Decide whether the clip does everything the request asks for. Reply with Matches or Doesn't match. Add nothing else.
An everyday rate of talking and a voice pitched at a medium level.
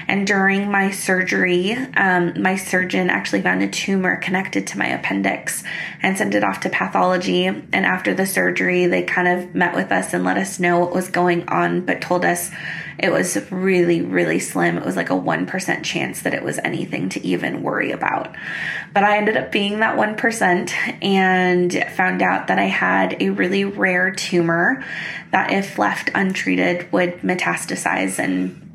Matches